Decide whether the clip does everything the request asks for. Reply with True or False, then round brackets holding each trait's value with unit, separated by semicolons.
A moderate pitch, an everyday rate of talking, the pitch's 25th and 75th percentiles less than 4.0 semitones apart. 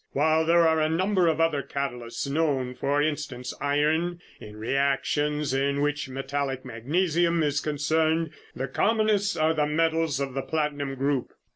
True (150 Hz; 150 wpm; 2.8 semitones)